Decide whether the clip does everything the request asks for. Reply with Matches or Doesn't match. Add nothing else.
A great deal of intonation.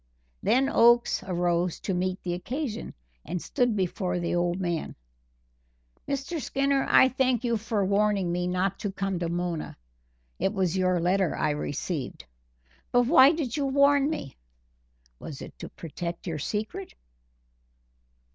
Matches